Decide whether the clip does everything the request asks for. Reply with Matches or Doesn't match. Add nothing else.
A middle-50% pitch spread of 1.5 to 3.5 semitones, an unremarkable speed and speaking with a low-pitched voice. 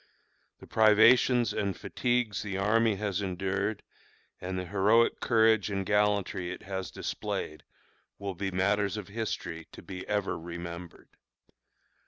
Doesn't match